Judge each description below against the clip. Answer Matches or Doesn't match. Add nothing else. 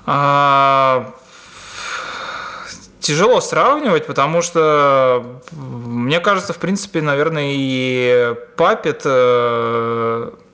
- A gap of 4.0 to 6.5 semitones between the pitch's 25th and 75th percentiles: Matches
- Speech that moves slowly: Matches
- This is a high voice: Doesn't match